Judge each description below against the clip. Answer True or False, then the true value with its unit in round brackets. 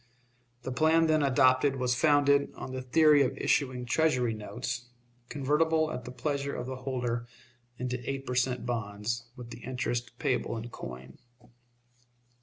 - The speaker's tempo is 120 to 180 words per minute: True (150 wpm)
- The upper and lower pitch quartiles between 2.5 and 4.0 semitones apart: True (2.8 semitones)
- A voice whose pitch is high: False (125 Hz)